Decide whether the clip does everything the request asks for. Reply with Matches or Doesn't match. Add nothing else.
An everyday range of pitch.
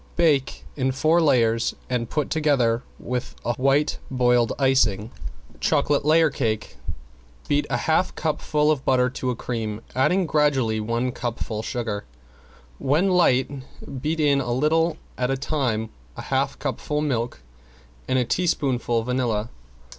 Matches